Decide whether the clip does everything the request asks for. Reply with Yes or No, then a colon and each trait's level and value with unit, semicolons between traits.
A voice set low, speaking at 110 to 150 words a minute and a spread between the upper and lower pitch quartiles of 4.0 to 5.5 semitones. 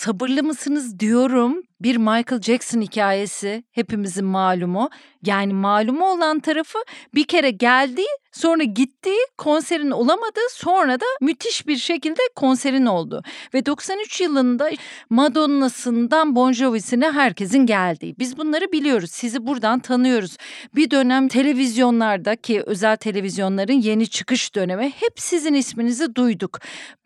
No: very high, 255 Hz; average, 120 wpm; average, 5.2 semitones